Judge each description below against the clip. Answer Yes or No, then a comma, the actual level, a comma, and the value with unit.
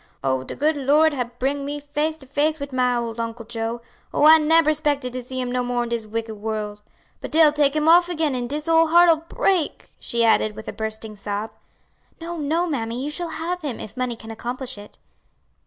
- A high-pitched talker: Yes, very high, 260 Hz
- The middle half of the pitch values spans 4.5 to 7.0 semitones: Yes, average, 5.1 semitones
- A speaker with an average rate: No, fast, 220 wpm